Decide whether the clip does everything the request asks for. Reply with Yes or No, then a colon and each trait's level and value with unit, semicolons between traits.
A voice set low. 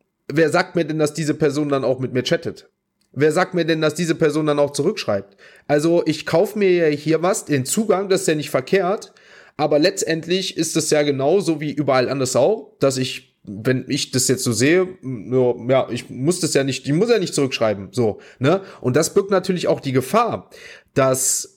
No: medium, 150 Hz